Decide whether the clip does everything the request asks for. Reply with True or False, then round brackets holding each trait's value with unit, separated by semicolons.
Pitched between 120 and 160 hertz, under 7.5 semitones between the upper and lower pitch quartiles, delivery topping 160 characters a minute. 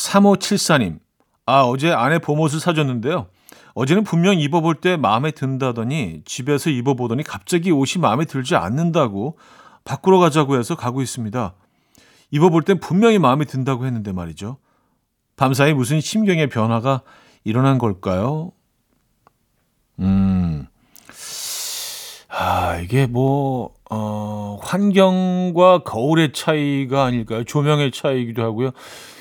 True (135 Hz; 6.0 semitones; 270 characters per minute)